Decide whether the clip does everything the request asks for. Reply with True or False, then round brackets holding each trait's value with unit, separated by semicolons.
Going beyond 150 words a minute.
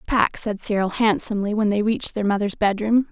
True (195 wpm)